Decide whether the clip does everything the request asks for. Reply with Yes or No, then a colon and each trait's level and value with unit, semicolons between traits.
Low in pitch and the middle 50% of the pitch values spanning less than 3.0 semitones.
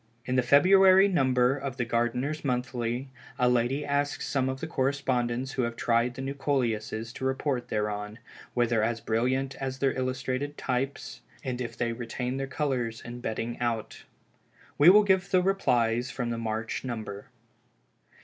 Yes: low, 125 Hz; narrow, 2.6 semitones